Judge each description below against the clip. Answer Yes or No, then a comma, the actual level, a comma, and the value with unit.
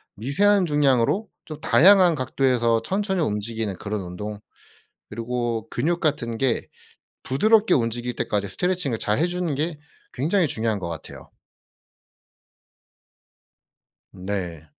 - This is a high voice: No, low, 125 Hz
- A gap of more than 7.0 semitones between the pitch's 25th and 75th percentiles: Yes, wide, 7.8 semitones